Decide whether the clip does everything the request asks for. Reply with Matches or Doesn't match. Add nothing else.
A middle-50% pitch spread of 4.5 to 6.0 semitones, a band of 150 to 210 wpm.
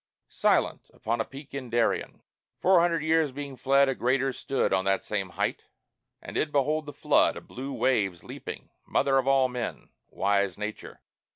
Doesn't match